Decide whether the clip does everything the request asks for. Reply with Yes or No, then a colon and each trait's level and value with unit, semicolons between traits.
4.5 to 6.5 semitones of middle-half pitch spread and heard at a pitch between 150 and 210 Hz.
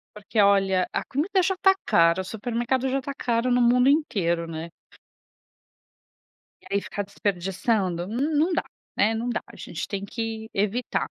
No: average, 4.8 semitones; high, 225 Hz